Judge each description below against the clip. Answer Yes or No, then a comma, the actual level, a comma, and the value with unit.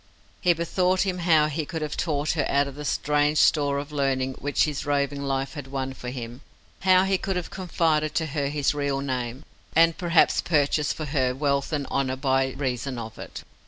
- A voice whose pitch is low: No, medium, 145 Hz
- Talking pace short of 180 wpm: No, average, 200 wpm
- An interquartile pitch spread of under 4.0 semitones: Yes, average, 2.7 semitones